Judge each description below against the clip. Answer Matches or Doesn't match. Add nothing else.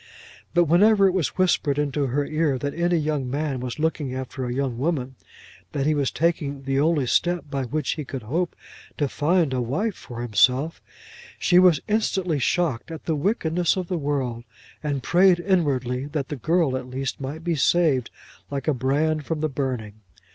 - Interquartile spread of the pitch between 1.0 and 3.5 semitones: Doesn't match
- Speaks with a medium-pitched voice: Matches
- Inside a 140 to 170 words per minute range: Doesn't match